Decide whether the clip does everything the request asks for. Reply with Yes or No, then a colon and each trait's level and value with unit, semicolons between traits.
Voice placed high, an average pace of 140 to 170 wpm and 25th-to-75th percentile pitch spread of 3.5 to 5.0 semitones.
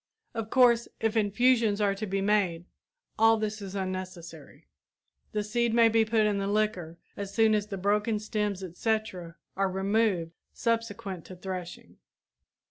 No: high, 205 Hz; average, 150 wpm; average, 2.8 semitones